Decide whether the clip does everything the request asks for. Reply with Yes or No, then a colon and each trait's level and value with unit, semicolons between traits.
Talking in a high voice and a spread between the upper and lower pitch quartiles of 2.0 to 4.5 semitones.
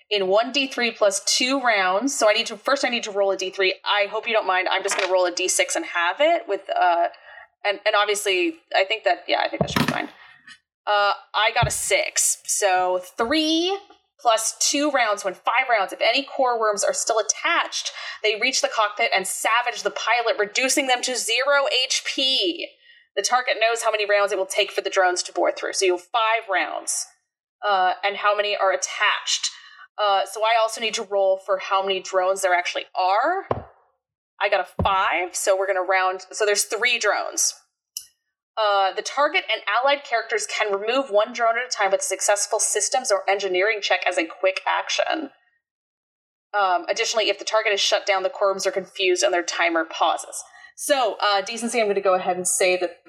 No: high, 210 Hz; average, 4.9 semitones